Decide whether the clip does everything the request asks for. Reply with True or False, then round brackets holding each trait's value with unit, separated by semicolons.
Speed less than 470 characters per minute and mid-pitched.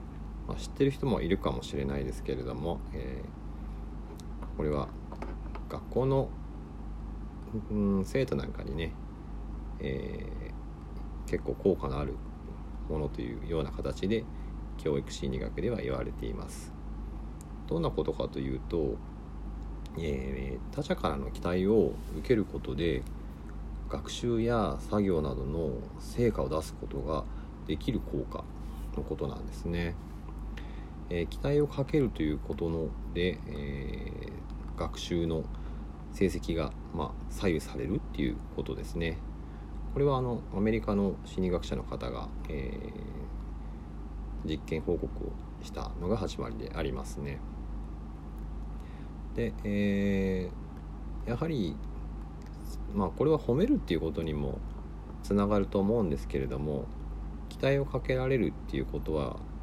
False (240 characters per minute; 75 Hz)